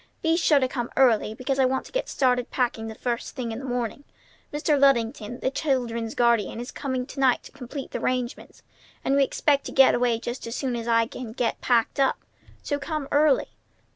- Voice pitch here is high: Yes, very high, 255 Hz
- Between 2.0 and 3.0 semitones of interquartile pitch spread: Yes, narrow, 2.6 semitones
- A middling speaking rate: No, fast, 210 wpm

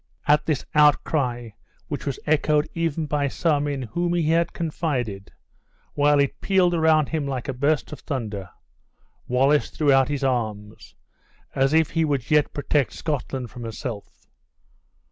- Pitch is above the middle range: No, medium, 145 Hz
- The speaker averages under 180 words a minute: Yes, average, 150 wpm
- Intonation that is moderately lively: Yes, average, 3.4 semitones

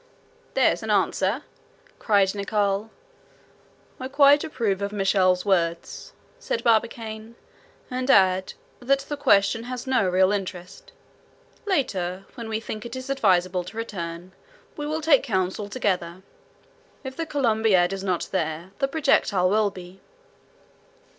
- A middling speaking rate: No, slow, 130 wpm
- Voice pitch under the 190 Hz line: No, high, 205 Hz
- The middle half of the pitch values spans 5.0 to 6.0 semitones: Yes, wide, 5.4 semitones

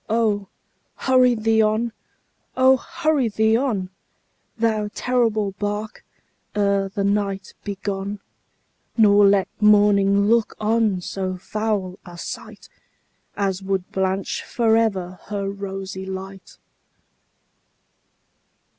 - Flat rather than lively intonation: Yes, narrow, 2.3 semitones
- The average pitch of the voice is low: No, high, 205 Hz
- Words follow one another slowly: Yes, slow, 105 wpm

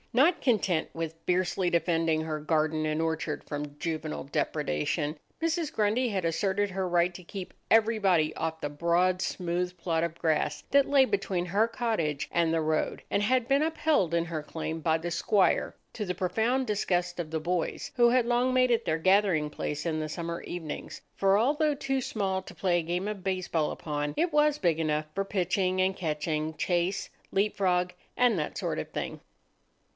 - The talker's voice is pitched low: No, medium, 180 Hz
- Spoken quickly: No, average, 185 wpm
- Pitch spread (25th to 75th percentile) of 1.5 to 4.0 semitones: No, average, 4.5 semitones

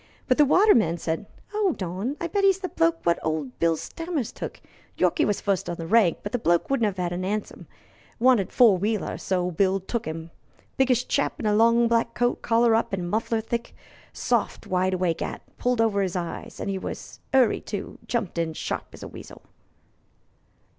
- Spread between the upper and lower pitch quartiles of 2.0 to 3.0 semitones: No, average, 5.3 semitones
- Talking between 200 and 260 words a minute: Yes, fast, 205 wpm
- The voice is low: No, high, 210 Hz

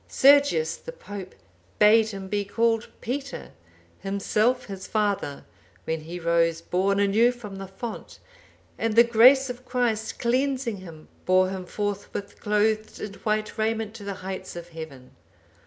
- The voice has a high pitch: Yes, high, 210 Hz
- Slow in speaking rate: No, average, 145 wpm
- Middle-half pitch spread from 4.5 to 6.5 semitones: No, average, 3.6 semitones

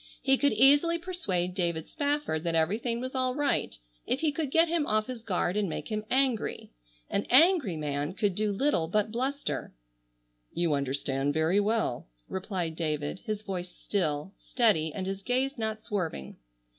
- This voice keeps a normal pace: Yes, average, 165 wpm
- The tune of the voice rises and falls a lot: Yes, wide, 7.4 semitones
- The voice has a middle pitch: No, high, 210 Hz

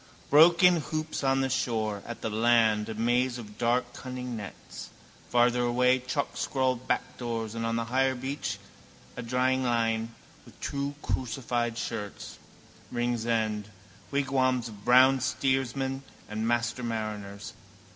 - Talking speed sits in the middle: No, slow, 125 wpm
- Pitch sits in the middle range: No, low, 120 Hz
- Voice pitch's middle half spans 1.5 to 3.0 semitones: Yes, narrow, 2.5 semitones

